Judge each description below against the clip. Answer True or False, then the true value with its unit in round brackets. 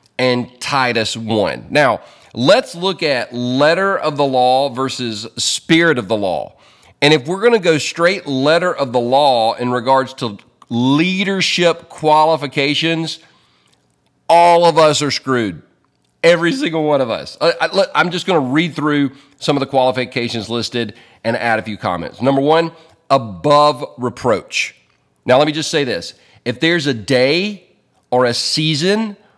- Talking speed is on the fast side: False (155 wpm)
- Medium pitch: True (145 Hz)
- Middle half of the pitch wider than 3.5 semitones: True (4.9 semitones)